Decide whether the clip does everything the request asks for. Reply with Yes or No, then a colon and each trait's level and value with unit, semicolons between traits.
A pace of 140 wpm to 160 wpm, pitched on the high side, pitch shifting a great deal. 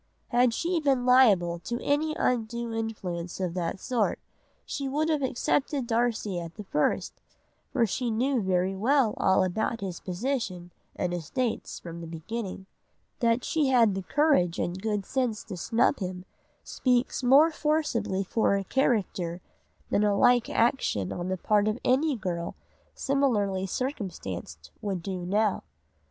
Yes: average, 150 wpm; high, 220 Hz; wide, 5.7 semitones